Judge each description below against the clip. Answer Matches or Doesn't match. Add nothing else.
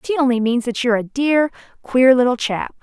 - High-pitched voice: Matches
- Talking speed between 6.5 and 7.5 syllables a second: Doesn't match